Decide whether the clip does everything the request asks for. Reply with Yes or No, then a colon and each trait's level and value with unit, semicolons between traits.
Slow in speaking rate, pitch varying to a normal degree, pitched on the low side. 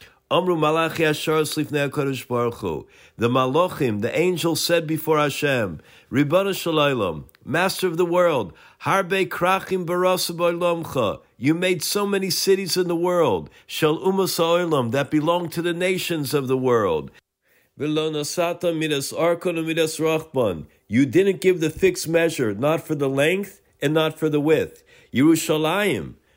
No: slow, 115 wpm; average, 3.3 semitones; medium, 165 Hz